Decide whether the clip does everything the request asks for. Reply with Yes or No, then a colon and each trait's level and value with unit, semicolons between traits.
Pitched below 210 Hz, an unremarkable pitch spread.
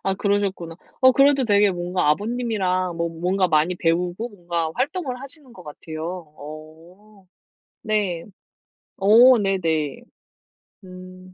Yes: medium, 185 Hz; average, 4.1 semitones